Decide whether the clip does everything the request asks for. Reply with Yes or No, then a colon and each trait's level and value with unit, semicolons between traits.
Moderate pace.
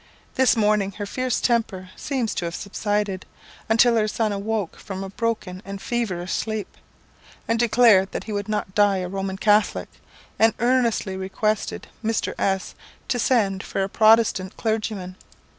Yes: average, 155 wpm